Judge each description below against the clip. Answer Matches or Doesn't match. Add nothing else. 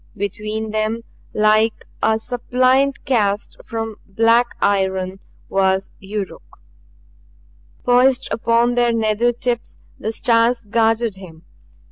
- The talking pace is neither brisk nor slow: Doesn't match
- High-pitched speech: Matches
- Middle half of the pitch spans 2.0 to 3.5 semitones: Matches